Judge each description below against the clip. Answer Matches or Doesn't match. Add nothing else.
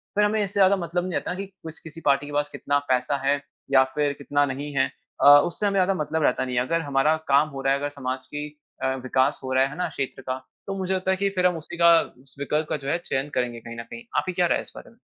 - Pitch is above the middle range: Doesn't match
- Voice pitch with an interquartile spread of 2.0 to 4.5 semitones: Doesn't match